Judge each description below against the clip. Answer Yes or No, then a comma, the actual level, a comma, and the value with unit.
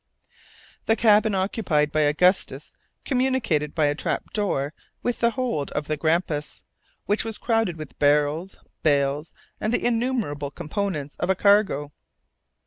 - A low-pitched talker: No, medium, 175 Hz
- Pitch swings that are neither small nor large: No, wide, 6.8 semitones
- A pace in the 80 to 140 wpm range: Yes, slow, 135 wpm